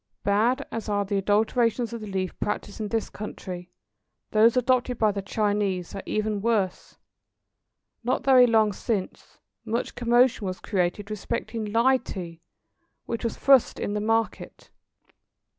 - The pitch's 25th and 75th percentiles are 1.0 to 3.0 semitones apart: Yes, narrow, 2.6 semitones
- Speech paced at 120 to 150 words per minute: Yes, average, 140 wpm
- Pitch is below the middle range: No, high, 215 Hz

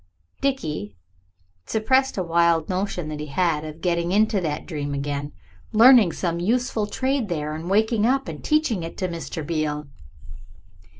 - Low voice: No, medium, 175 Hz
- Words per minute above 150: No, average, 145 wpm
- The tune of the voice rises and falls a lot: Yes, wide, 6.1 semitones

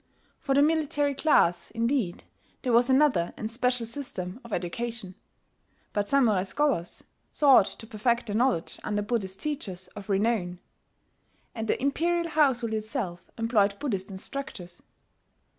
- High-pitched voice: Yes, high, 230 Hz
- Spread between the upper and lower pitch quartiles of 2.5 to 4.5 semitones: No, wide, 5.6 semitones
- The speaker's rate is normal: No, slow, 130 wpm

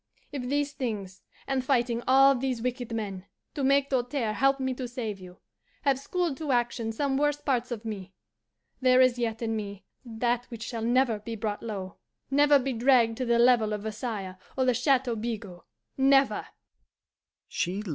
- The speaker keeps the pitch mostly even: No, average, 3.3 semitones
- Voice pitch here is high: Yes, high, 245 Hz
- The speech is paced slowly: No, average, 170 wpm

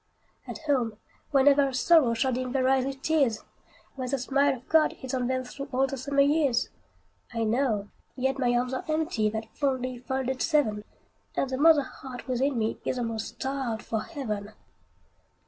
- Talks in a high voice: Yes, very high, 260 Hz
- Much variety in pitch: No, narrow, 2.6 semitones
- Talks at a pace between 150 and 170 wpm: No, average, 180 wpm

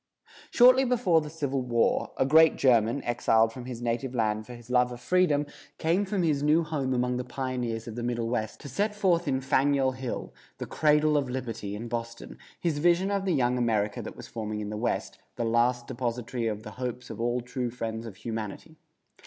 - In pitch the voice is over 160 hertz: No, low, 125 Hz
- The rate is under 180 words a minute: No, fast, 205 wpm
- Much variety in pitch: No, average, 4.3 semitones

